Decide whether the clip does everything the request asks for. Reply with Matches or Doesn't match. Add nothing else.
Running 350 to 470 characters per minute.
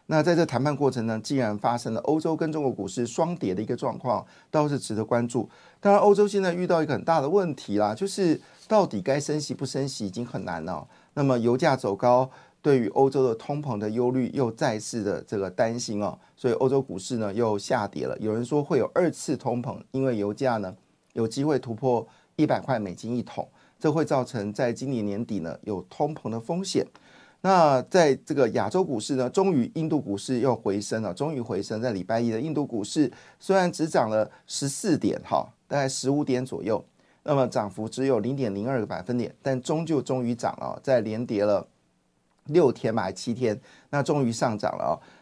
Doesn't match